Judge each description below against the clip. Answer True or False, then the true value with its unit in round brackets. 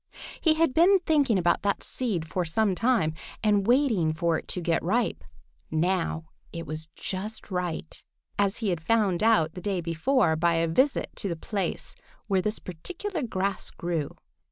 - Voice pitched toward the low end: False (190 Hz)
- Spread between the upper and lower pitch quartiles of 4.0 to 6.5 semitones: True (5.4 semitones)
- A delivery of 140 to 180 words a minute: True (170 wpm)